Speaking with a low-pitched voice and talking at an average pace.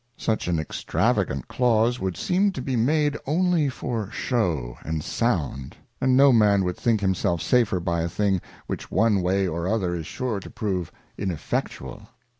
Yes: low, 100 Hz; average, 165 wpm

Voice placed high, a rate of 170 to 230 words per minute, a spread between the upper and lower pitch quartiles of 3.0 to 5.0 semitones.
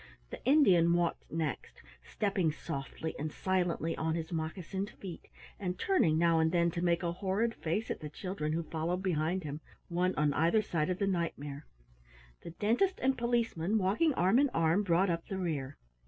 No: medium, 170 Hz; average, 185 wpm; average, 3.4 semitones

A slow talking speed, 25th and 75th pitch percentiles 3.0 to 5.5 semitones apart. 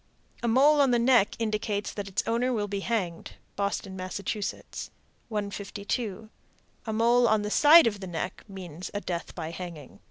No: average, 165 wpm; average, 3.6 semitones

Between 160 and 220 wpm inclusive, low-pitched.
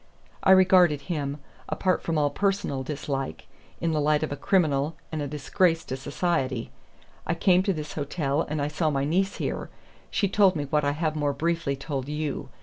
No: average, 190 wpm; medium, 150 Hz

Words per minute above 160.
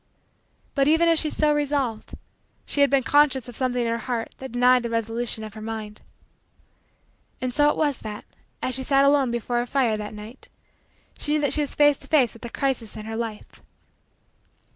Yes: fast, 205 wpm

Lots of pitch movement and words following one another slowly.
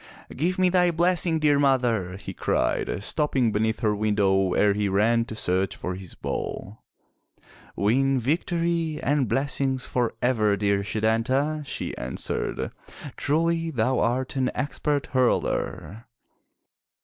Yes: wide, 6.0 semitones; slow, 125 wpm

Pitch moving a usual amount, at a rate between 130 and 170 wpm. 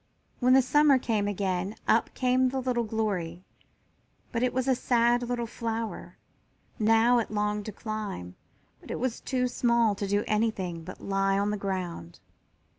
Yes: average, 3.5 semitones; average, 165 wpm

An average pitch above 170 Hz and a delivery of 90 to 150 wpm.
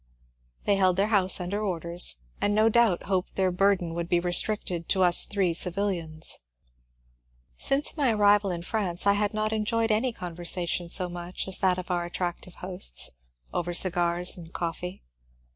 No: medium, 185 Hz; average, 160 wpm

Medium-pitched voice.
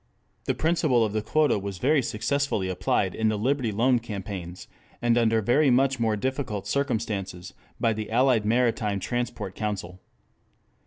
No: low, 110 Hz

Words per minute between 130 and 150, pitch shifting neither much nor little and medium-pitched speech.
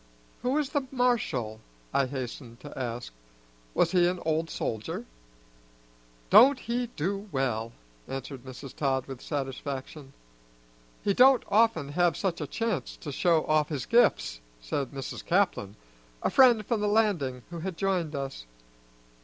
No: average, 145 wpm; wide, 7.7 semitones; medium, 155 Hz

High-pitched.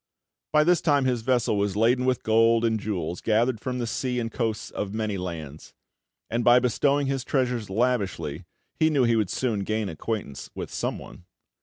No: low, 115 Hz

